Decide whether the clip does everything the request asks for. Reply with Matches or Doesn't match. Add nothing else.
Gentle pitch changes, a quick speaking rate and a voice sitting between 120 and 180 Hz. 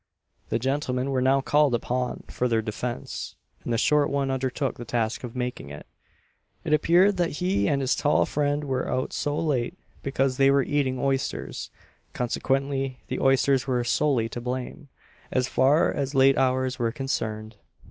Doesn't match